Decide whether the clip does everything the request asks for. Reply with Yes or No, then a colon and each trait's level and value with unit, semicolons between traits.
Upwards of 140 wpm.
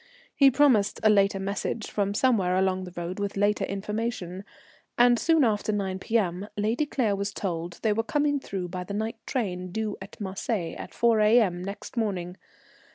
Yes: average, 175 wpm